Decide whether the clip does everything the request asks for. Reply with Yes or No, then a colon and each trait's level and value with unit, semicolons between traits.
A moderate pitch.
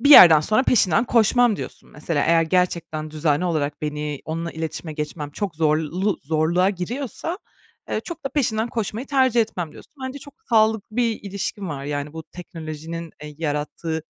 Yes: medium, 170 Hz